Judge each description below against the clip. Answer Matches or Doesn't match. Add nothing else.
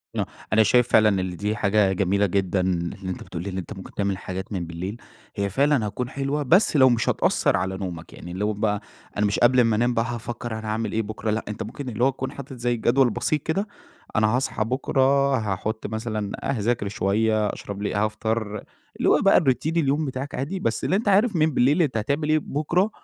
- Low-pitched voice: Matches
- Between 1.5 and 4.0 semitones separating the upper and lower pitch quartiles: Doesn't match